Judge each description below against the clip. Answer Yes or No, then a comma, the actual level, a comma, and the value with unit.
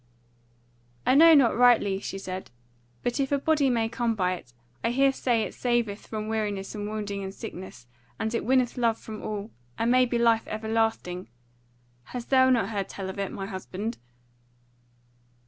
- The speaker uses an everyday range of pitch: Yes, average, 3.5 semitones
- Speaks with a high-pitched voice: Yes, high, 225 Hz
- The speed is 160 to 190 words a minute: Yes, average, 170 wpm